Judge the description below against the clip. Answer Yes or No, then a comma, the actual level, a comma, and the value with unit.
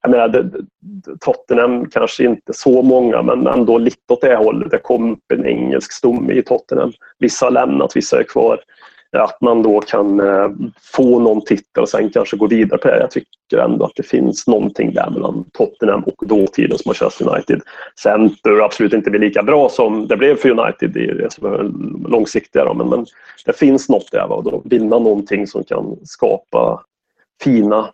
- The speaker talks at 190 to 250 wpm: No, average, 175 wpm